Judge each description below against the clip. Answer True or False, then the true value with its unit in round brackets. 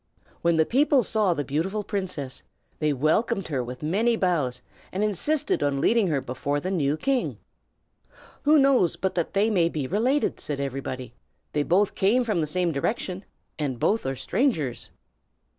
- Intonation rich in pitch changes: True (6.9 semitones)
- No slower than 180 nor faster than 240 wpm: False (165 wpm)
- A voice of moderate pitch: True (175 Hz)